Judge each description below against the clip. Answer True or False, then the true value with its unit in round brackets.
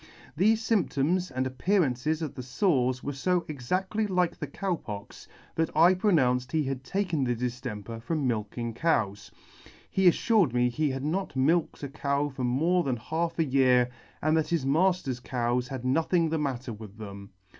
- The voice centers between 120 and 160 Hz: True (140 Hz)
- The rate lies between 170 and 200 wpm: True (175 wpm)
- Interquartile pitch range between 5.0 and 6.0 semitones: True (5.4 semitones)